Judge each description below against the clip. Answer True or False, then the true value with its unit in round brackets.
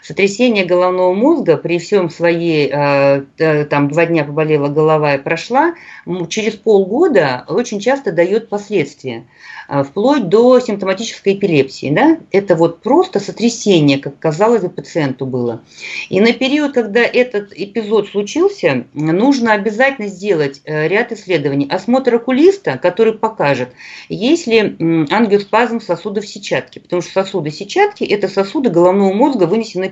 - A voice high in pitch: True (195 Hz)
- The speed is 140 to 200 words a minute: False (125 wpm)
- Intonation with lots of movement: True (5.9 semitones)